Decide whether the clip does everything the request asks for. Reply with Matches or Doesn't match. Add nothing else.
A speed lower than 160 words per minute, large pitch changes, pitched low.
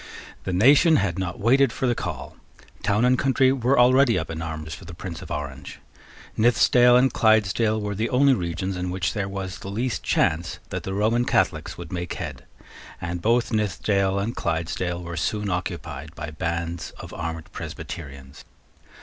Doesn't match